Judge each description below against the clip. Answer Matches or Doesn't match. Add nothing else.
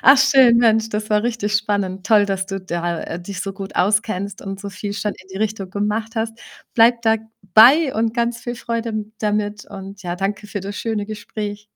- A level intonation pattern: Matches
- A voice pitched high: Matches